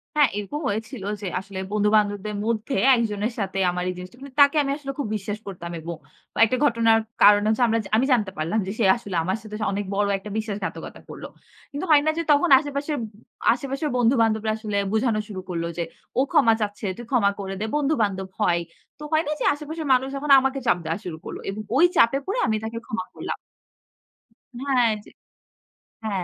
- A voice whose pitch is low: No, high, 220 Hz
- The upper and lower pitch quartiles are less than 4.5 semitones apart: No, average, 5.0 semitones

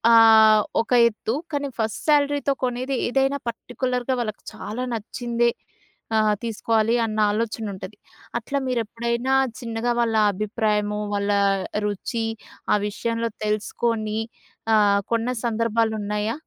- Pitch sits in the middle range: No, high, 225 Hz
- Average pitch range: No, narrow, 2.0 semitones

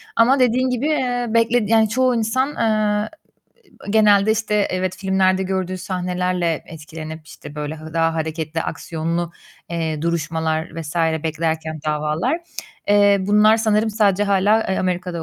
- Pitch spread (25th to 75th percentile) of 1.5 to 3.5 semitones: No, average, 5.1 semitones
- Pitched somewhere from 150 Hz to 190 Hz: Yes, medium, 185 Hz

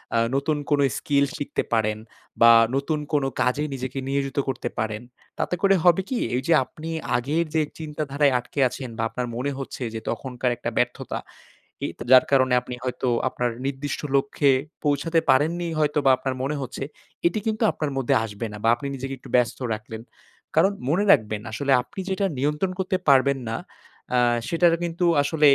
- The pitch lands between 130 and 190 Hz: Yes, medium, 140 Hz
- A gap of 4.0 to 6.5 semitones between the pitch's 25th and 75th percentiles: No, average, 3.5 semitones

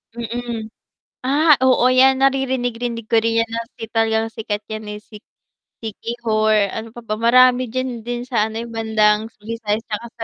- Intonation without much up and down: Yes, narrow, 1.8 semitones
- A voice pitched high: Yes, high, 230 Hz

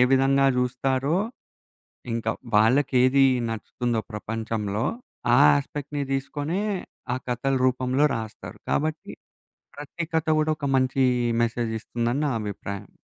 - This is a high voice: No, low, 130 Hz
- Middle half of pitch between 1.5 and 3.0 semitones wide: No, average, 3.7 semitones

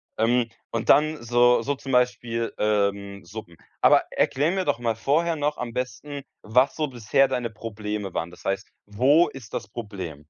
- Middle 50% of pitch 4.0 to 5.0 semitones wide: Yes, average, 4.5 semitones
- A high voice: No, low, 120 Hz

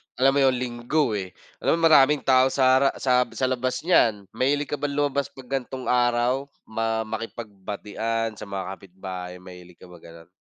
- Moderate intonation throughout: Yes, average, 4.7 semitones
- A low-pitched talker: Yes, low, 120 Hz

